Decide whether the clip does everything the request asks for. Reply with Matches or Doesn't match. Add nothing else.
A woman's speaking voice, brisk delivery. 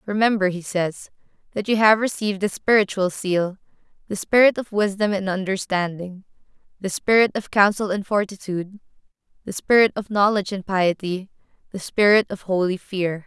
Doesn't match